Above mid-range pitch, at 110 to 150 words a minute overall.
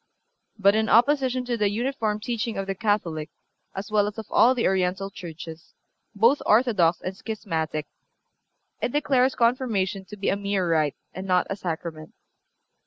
No: high, 205 Hz; average, 160 wpm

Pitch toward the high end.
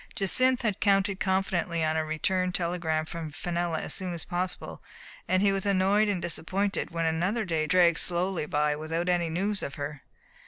No: medium, 175 Hz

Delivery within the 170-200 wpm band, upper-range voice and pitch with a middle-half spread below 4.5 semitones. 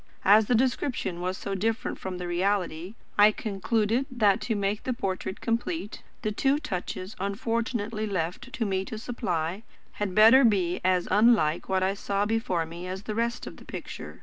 Yes: average, 175 wpm; high, 205 Hz; average, 3.6 semitones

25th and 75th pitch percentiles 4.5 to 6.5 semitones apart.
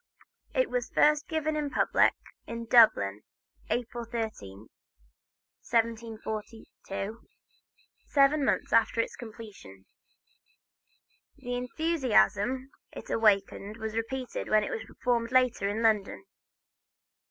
No: average, 3.0 semitones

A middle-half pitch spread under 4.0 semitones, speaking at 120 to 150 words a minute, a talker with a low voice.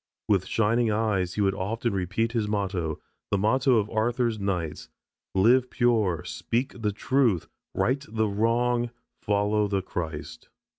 Yes: average, 3.4 semitones; average, 140 wpm; low, 105 Hz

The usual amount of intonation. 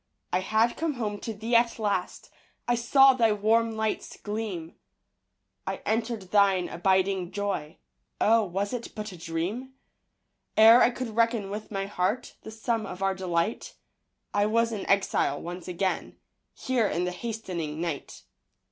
Yes: average, 3.6 semitones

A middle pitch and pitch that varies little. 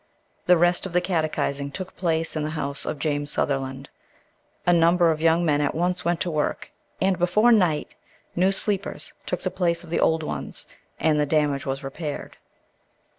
No: medium, 165 Hz; average, 3.2 semitones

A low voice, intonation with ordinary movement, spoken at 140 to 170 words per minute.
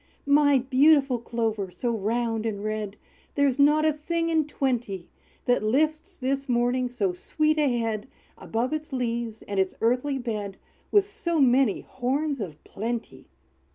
No: very high, 250 Hz; average, 4.5 semitones; average, 155 wpm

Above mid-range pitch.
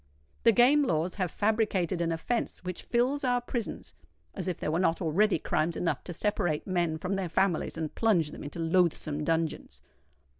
No: medium, 180 Hz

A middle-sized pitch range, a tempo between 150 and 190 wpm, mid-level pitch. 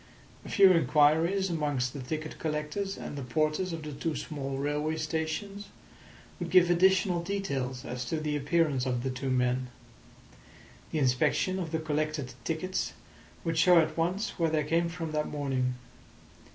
Yes: average, 3.4 semitones; average, 160 wpm; medium, 155 Hz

